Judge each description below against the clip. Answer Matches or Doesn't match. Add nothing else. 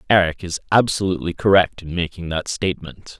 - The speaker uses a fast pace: Doesn't match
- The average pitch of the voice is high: Doesn't match